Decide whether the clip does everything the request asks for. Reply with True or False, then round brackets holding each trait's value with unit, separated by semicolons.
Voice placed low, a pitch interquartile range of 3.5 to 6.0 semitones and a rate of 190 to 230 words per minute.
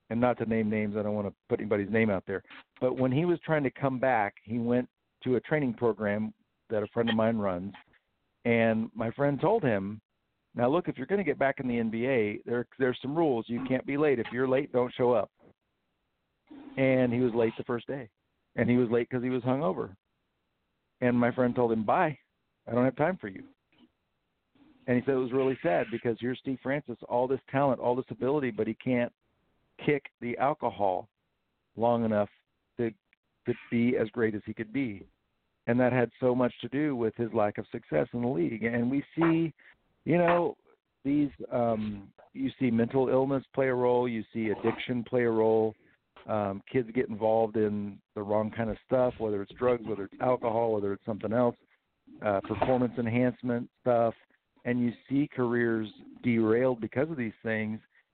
False (120 Hz; 2.6 semitones; 200 wpm)